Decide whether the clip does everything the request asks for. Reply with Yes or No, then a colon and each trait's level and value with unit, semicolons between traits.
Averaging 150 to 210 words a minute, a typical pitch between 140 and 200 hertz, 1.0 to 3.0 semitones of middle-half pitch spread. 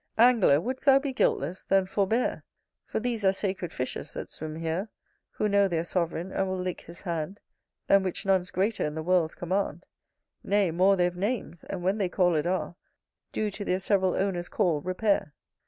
Yes: average, 185 wpm; medium, 185 Hz; narrow, 2.6 semitones